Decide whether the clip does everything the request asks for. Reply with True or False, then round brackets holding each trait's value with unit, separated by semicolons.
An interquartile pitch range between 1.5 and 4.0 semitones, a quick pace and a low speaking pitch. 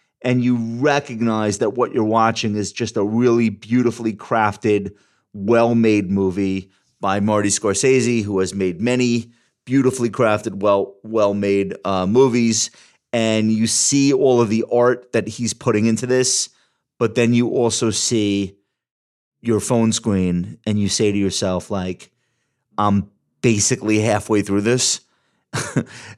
False (2.9 semitones; 140 wpm; 110 Hz)